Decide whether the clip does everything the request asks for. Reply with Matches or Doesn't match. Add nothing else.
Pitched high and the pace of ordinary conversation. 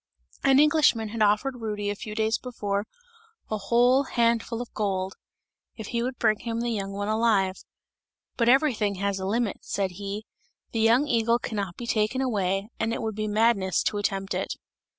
Matches